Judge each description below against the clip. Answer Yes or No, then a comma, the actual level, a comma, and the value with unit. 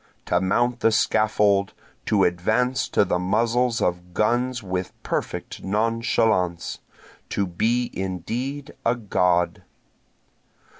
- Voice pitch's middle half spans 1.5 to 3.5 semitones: No, average, 4.6 semitones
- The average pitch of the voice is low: Yes, low, 105 Hz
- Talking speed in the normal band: No, slow, 105 wpm